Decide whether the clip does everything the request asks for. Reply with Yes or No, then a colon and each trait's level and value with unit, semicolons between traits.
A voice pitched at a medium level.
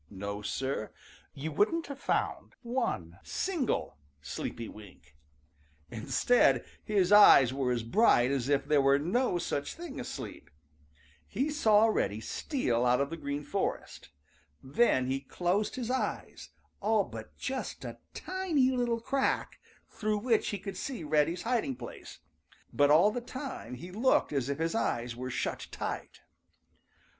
Yes: medium, 165 Hz